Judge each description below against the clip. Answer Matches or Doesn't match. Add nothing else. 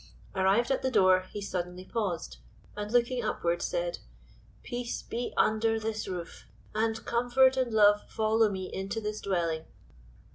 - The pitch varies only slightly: Doesn't match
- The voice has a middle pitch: Doesn't match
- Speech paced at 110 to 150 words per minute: Matches